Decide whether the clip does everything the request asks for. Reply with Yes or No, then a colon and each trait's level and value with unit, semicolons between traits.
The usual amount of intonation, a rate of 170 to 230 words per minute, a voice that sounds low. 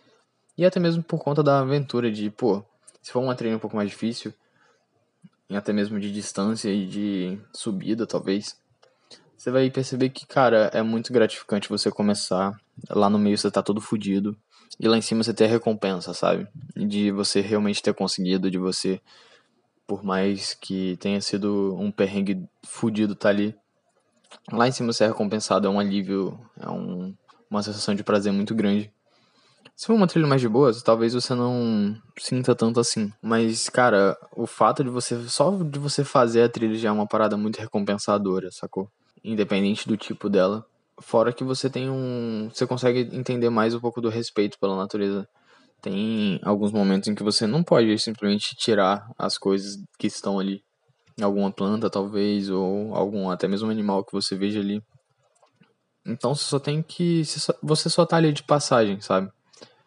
Yes: average, 3.4 semitones; average, 175 wpm; low, 110 Hz